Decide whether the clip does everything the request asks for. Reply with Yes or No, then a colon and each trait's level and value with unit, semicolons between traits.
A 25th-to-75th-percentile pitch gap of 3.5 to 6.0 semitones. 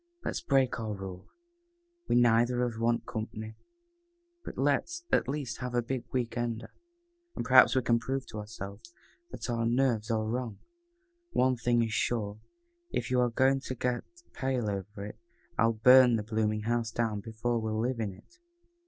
No: narrow, 2.4 semitones